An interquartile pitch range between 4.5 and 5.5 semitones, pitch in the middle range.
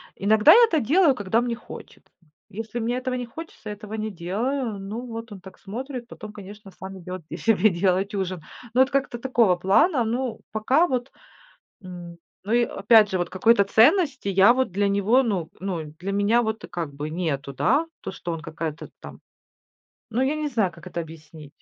No: average, 4.8 semitones; high, 210 Hz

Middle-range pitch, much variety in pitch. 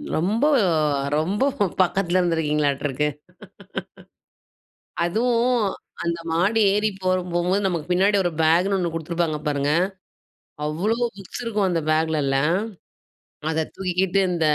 No: medium, 175 Hz; average, 3.6 semitones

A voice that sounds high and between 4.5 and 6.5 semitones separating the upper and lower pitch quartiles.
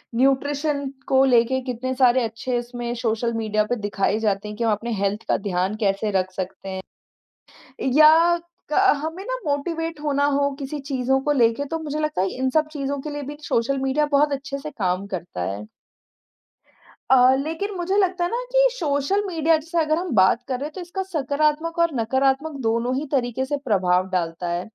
Yes: very high, 270 Hz; average, 5.2 semitones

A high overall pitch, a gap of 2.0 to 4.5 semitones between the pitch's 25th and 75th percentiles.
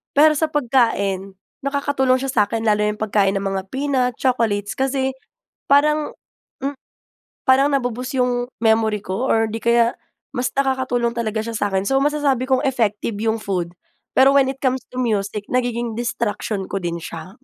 Yes: high, 240 Hz; average, 4.1 semitones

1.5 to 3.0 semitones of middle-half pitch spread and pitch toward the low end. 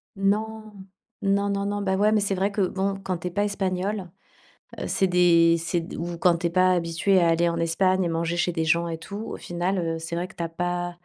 No: average, 2.7 semitones; medium, 180 Hz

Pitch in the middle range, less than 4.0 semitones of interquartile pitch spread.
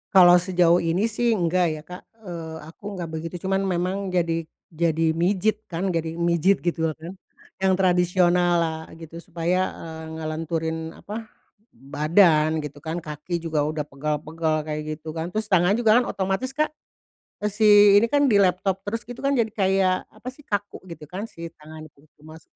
Yes: medium, 175 Hz; average, 3.4 semitones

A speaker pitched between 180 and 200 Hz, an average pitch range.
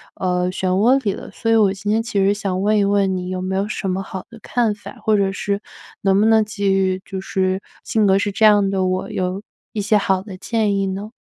No: high, 195 Hz; narrow, 1.9 semitones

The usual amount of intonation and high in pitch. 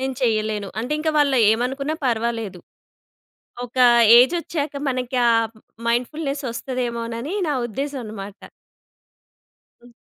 Yes: average, 3.3 semitones; very high, 250 Hz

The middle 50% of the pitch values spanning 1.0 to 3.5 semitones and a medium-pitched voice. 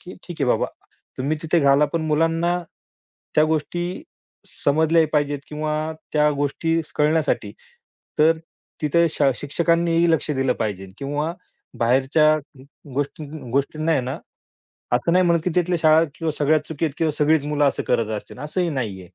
Yes: average, 2.7 semitones; medium, 155 Hz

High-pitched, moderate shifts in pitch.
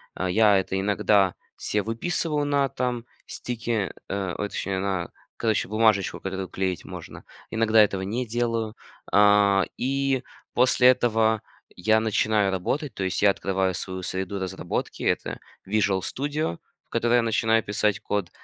No: low, 105 Hz; average, 3.4 semitones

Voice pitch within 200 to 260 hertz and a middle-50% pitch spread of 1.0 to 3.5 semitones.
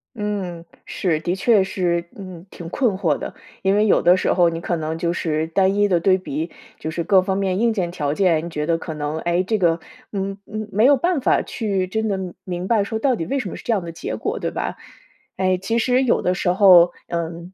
No: medium, 185 Hz; average, 3.2 semitones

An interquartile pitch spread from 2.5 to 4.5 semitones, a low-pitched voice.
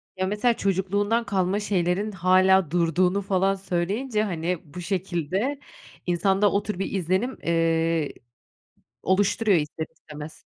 No: average, 2.9 semitones; high, 190 Hz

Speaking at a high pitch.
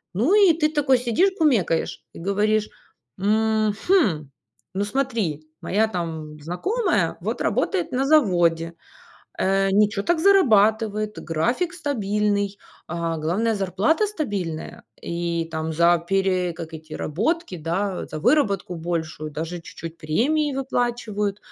Yes: high, 200 Hz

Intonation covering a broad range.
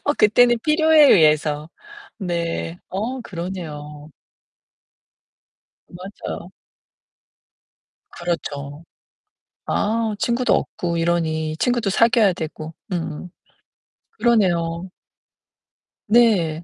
Yes: wide, 6.2 semitones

